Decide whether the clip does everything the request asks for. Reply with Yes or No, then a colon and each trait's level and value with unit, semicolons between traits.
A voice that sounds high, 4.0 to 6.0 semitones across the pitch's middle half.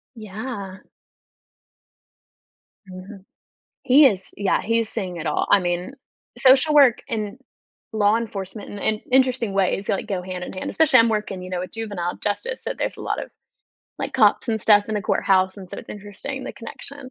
No: high, 210 Hz; average, 3.6 semitones